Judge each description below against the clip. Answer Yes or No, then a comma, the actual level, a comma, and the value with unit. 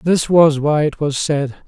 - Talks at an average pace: No, fast, 215 wpm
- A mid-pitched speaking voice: Yes, medium, 150 Hz